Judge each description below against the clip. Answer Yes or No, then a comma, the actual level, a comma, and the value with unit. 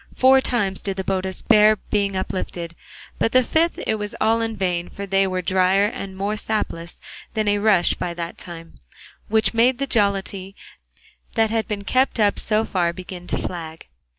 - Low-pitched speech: No, high, 200 Hz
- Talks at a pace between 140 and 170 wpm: No, average, 180 wpm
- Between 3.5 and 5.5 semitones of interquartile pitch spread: No, average, 2.9 semitones